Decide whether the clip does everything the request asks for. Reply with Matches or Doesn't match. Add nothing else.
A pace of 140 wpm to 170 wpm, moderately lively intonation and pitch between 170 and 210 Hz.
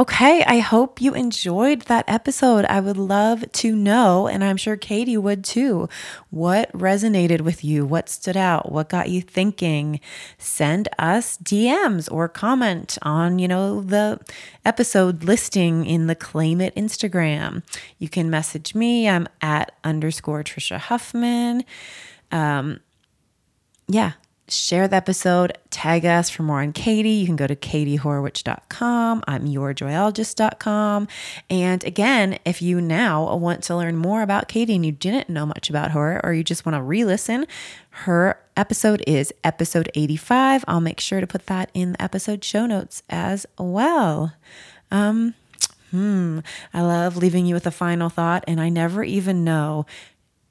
Matches